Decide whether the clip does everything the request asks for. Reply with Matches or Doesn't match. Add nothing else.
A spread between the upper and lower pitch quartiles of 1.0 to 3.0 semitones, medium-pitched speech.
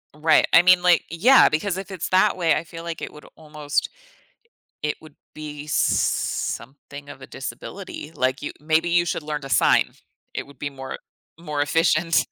Matches